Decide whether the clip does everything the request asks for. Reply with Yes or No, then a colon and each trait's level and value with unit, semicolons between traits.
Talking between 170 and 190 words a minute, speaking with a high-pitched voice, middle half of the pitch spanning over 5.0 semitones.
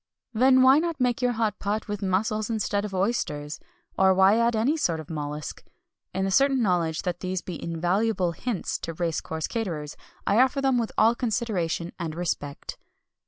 Yes: average, 180 wpm; high, 200 Hz; wide, 5.5 semitones